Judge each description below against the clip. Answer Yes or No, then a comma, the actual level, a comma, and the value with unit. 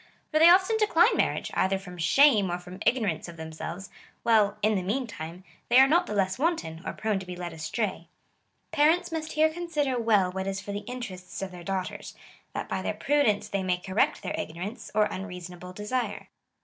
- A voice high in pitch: Yes, high, 200 Hz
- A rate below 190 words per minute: No, average, 200 wpm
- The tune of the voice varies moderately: No, wide, 6.3 semitones